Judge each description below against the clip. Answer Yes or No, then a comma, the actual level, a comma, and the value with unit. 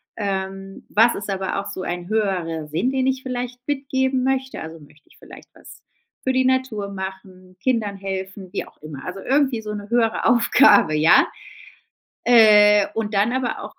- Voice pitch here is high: Yes, high, 210 Hz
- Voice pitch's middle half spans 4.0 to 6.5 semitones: Yes, average, 4.8 semitones